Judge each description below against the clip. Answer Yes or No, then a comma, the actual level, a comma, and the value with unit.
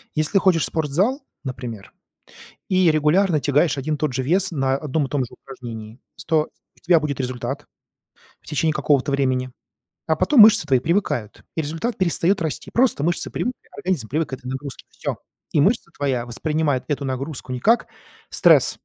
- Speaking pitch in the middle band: Yes, medium, 150 Hz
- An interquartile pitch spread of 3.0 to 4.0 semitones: No, average, 4.4 semitones